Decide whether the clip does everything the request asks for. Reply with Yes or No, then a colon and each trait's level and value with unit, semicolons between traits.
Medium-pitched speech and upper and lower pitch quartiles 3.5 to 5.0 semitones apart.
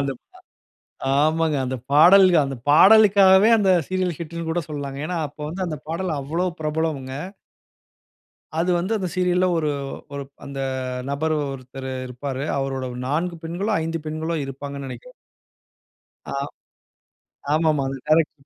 Yes: medium, 160 Hz; average, 4.2 semitones